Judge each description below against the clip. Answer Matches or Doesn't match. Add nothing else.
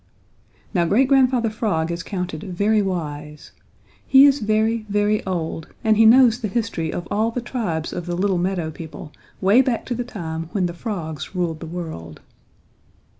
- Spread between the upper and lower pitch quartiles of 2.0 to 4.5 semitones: Doesn't match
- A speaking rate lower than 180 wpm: Matches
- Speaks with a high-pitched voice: Matches